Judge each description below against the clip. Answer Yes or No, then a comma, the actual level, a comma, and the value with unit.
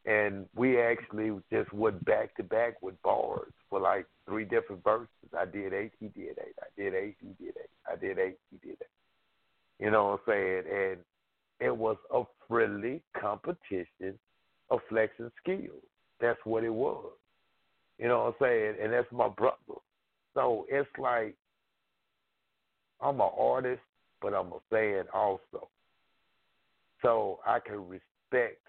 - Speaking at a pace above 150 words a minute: Yes, average, 165 wpm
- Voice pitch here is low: Yes, low, 125 Hz